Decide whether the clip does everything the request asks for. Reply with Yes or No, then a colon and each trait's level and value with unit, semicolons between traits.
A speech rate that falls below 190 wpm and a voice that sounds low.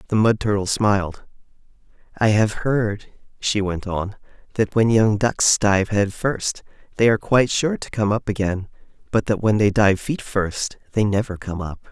Yes: average, 180 wpm; low, 105 Hz